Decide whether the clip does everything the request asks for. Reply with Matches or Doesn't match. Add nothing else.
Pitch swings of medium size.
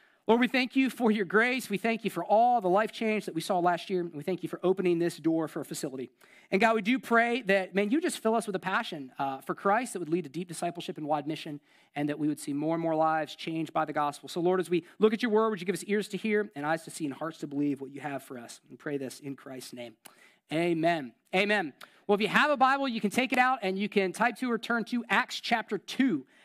Doesn't match